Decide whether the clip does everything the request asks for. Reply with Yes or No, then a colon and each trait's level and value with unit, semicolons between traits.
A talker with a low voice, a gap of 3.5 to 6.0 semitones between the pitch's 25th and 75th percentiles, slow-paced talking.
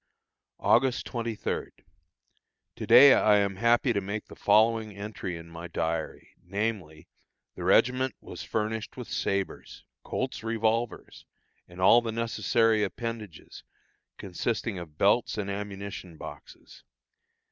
No: low, 105 Hz; average, 3.0 semitones; slow, 120 wpm